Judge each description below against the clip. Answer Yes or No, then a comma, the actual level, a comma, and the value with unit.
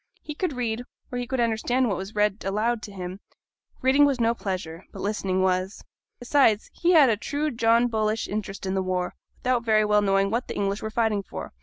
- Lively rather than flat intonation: No, average, 3.7 semitones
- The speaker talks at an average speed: No, fast, 210 wpm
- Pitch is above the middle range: Yes, high, 220 Hz